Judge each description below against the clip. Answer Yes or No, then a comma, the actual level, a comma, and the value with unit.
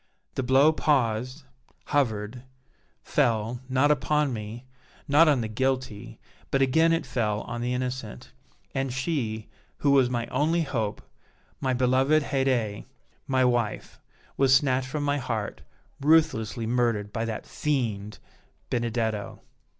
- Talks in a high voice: No, low, 125 Hz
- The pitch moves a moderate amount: Yes, average, 3.6 semitones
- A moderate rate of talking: No, slow, 125 wpm